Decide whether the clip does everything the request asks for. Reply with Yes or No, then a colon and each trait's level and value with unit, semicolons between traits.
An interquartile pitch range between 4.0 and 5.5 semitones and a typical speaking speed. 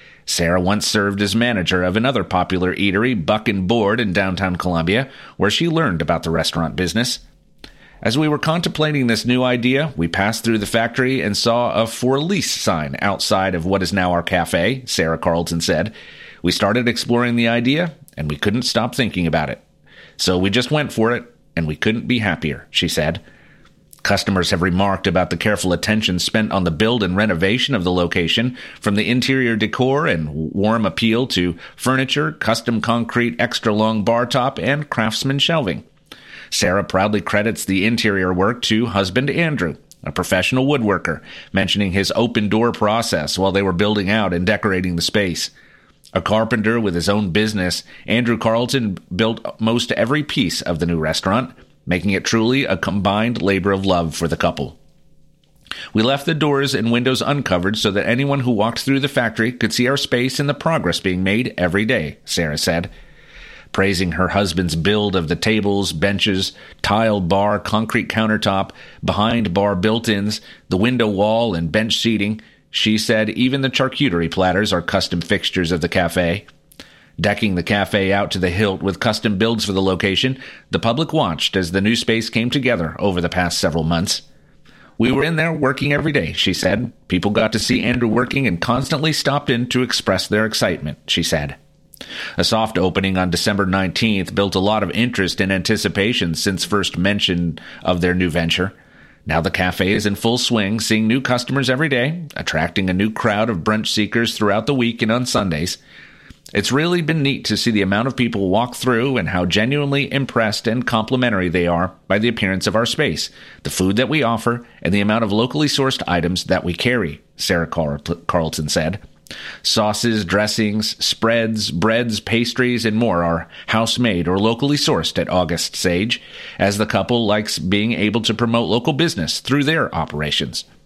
Yes: average, 4.5 semitones; average, 180 wpm